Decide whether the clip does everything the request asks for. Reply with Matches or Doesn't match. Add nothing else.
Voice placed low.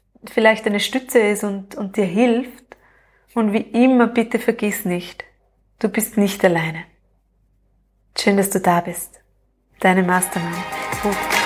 Doesn't match